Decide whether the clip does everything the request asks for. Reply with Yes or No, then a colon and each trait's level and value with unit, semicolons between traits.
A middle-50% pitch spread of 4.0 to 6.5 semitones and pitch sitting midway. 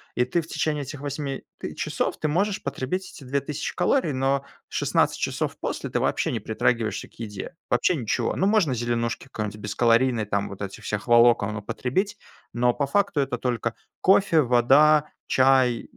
No: average, 4.5 semitones; low, 130 Hz